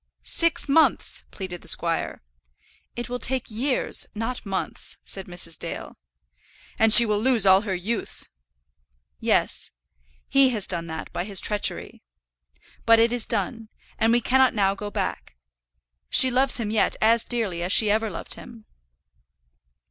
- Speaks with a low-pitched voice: No, high, 220 Hz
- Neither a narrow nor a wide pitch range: Yes, average, 3.9 semitones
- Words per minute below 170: Yes, average, 155 wpm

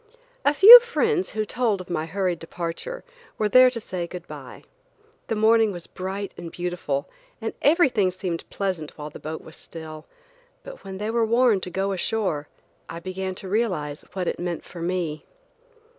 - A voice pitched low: No, medium, 185 Hz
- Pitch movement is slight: No, average, 4.7 semitones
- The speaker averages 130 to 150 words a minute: No, average, 180 wpm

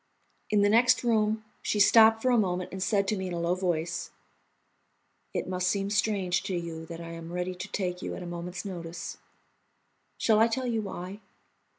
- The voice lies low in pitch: No, high, 190 Hz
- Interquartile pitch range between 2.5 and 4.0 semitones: Yes, average, 3.4 semitones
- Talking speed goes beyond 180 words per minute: Yes, average, 200 wpm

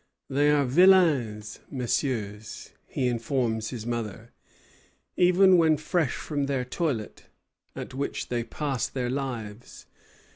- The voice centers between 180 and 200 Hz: No, low, 130 Hz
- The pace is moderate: No, slow, 115 wpm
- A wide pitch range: No, average, 4.3 semitones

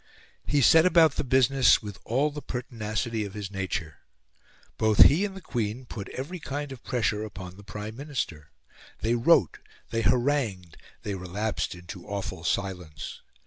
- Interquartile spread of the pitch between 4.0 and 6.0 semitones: Yes, wide, 5.5 semitones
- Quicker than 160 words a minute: No, average, 155 wpm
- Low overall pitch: Yes, low, 110 Hz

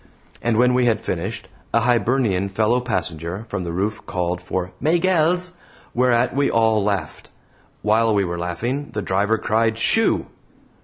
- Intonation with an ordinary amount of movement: Yes, average, 4.6 semitones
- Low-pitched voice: Yes, low, 110 Hz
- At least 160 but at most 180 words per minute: No, average, 150 wpm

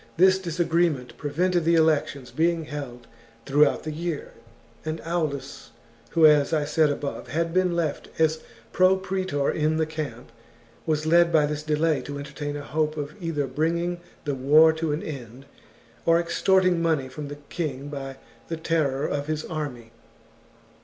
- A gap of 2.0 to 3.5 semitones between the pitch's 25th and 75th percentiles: Yes, narrow, 2.6 semitones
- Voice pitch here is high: No, medium, 155 Hz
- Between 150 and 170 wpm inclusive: Yes, average, 165 wpm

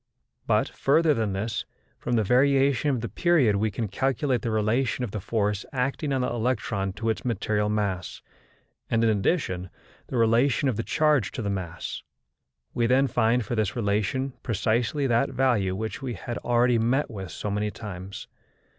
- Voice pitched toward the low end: Yes, low, 115 Hz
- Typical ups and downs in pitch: Yes, average, 3.9 semitones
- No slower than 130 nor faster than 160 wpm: No, average, 175 wpm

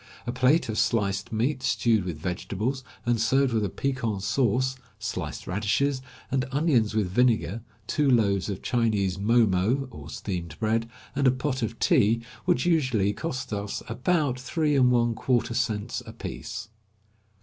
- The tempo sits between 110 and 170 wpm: Yes, average, 155 wpm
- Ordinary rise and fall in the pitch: Yes, average, 3.9 semitones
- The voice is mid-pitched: No, low, 115 Hz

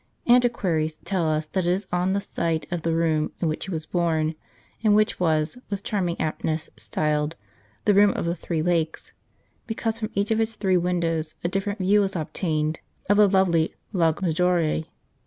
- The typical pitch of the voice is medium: Yes, medium, 175 Hz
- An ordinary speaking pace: Yes, average, 195 wpm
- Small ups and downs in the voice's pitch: No, average, 3.8 semitones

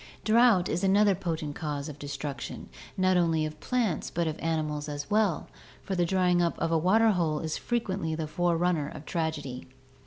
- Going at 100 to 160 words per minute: No, average, 175 wpm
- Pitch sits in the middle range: Yes, medium, 165 Hz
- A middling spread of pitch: Yes, average, 3.5 semitones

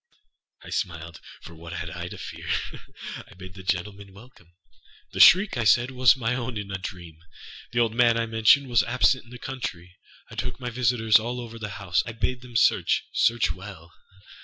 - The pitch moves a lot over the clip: No, average, 4.9 semitones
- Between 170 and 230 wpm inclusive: Yes, average, 185 wpm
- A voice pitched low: Yes, low, 110 Hz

